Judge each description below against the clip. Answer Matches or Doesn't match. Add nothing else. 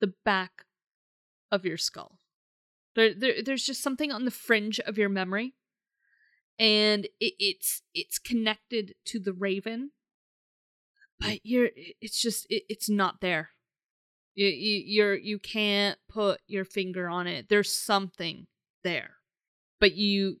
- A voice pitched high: Matches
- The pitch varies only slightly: Doesn't match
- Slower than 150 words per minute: Matches